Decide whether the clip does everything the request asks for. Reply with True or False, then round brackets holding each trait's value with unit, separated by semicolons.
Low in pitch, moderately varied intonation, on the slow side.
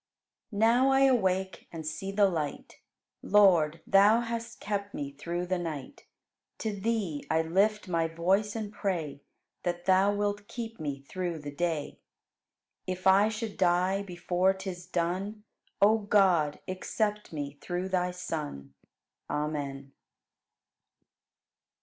False (185 Hz; 4.0 semitones; 130 wpm)